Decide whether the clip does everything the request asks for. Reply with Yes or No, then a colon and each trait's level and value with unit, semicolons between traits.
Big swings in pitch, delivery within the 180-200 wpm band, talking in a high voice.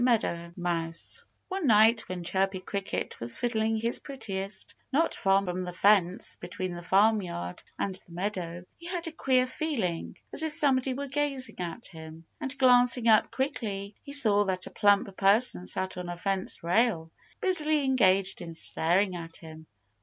No: wide, 6.2 semitones; average, 165 wpm; high, 200 Hz